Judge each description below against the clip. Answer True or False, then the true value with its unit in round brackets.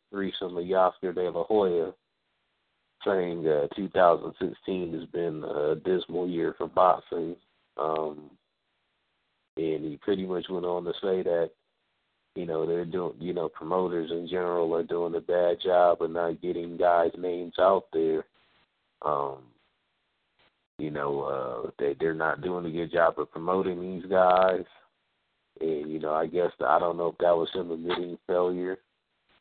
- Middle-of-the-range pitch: False (85 Hz)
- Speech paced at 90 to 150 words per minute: False (160 wpm)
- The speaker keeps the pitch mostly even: True (1.8 semitones)